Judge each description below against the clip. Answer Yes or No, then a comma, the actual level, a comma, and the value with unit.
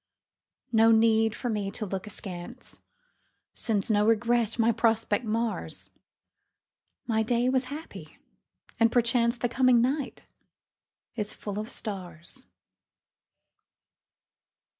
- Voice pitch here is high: Yes, high, 225 Hz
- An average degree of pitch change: No, narrow, 2.2 semitones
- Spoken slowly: Yes, slow, 105 wpm